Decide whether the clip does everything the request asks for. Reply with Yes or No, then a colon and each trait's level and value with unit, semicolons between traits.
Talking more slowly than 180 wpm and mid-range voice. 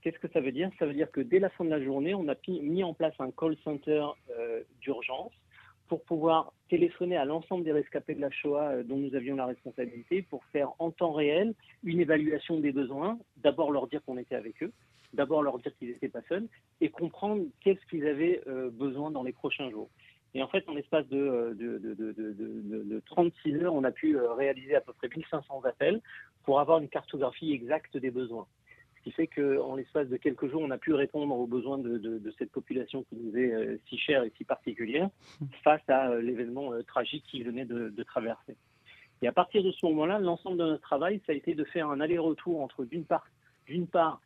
No: fast, 220 wpm; medium, 150 Hz